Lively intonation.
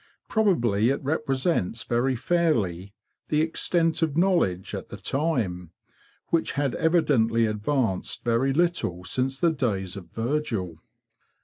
Yes: wide, 7.7 semitones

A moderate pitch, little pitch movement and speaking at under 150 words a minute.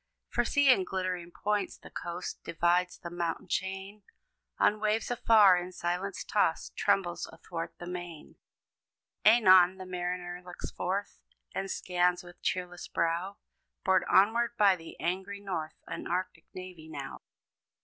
Yes: medium, 180 Hz; narrow, 1.9 semitones; average, 140 wpm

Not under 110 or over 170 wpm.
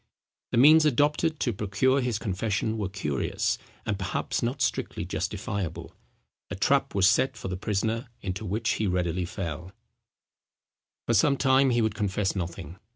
Yes: average, 155 wpm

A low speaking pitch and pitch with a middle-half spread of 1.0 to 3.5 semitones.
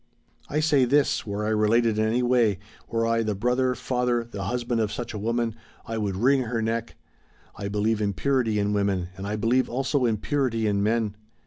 Yes: low, 115 Hz; average, 2.8 semitones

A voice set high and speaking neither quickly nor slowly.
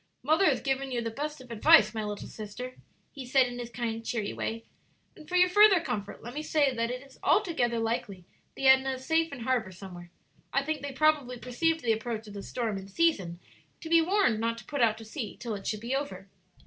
No: high, 245 Hz; fast, 230 wpm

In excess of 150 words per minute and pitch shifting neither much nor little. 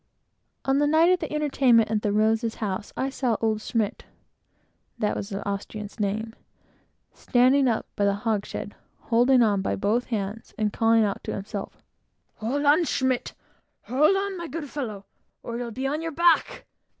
Yes: average, 170 wpm; average, 4.7 semitones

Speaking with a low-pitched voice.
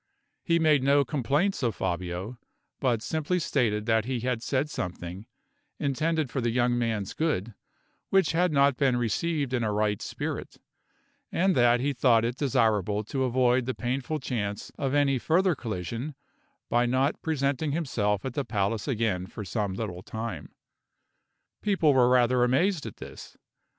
Yes: low, 125 Hz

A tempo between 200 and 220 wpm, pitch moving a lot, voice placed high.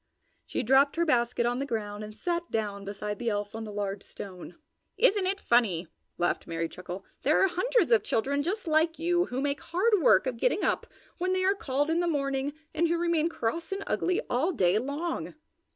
Yes: fast, 205 wpm; wide, 8.0 semitones; very high, 280 Hz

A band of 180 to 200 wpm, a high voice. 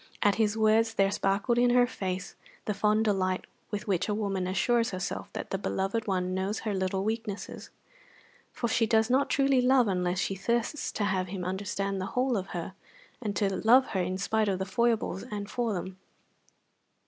Yes: average, 190 wpm; high, 205 Hz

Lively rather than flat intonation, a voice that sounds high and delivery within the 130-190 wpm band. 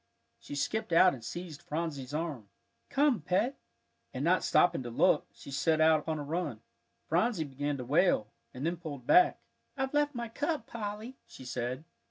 No: wide, 7.5 semitones; medium, 160 Hz; average, 175 wpm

